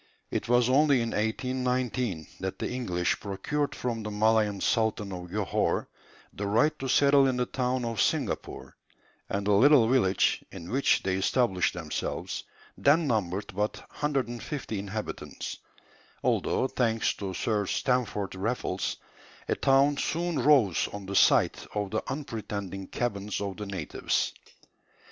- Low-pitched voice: Yes, low, 110 Hz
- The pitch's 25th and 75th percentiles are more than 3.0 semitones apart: Yes, average, 4.5 semitones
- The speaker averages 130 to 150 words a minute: Yes, average, 140 wpm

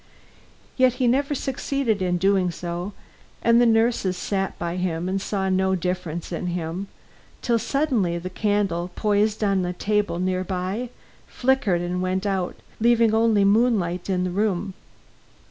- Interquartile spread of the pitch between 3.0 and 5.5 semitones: Yes, average, 3.7 semitones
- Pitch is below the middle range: No, high, 195 Hz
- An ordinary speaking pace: Yes, average, 145 wpm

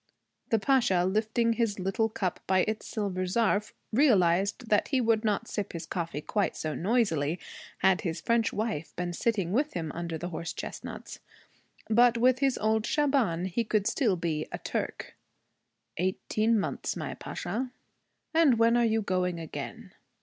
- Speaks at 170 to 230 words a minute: No, average, 160 wpm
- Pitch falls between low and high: No, high, 210 Hz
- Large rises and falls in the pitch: No, average, 4.5 semitones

